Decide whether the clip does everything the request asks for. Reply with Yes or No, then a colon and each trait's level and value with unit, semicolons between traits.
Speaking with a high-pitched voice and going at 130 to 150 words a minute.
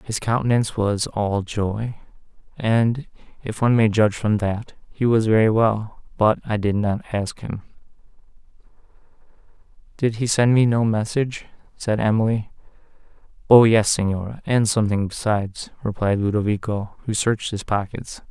No: low, 110 Hz; average, 140 wpm